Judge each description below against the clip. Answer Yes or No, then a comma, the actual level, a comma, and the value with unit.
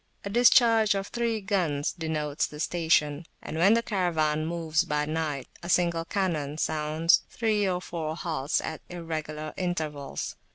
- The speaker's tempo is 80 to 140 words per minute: No, average, 150 wpm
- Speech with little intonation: No, average, 3.5 semitones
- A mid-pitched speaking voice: Yes, medium, 165 Hz